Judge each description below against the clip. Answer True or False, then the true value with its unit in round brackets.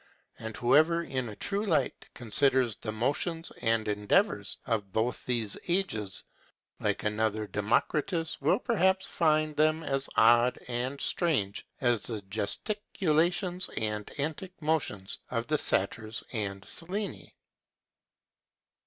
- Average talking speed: False (120 wpm)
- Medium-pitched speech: False (125 Hz)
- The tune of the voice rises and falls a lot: True (7.1 semitones)